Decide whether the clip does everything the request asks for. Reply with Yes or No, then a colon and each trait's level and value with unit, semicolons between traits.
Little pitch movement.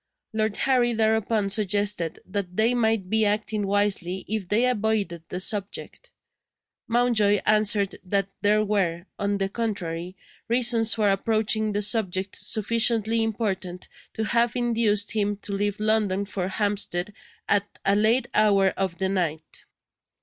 Yes: narrow, 2.2 semitones